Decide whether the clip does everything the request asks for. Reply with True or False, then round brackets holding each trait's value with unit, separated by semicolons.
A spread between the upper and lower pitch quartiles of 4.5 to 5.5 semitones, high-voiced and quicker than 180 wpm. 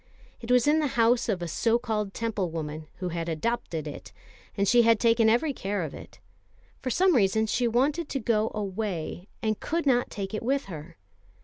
True (5.2 semitones; 220 Hz; 200 wpm)